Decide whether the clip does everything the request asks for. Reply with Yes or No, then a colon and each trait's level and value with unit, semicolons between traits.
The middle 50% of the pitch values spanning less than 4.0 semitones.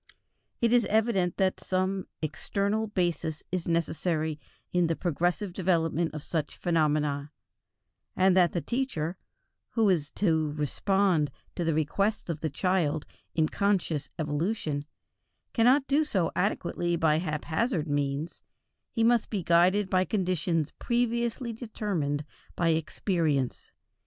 No: average, 4.5 semitones